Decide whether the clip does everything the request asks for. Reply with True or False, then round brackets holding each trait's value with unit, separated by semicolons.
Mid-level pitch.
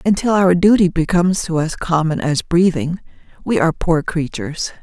True (170 Hz)